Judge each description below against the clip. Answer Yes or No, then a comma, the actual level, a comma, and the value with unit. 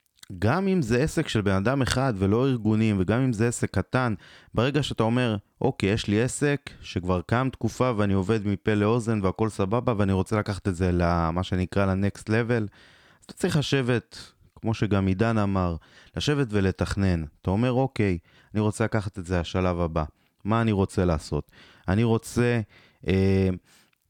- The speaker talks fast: Yes, fast, 165 wpm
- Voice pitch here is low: Yes, low, 105 Hz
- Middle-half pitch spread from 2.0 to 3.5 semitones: No, average, 4.1 semitones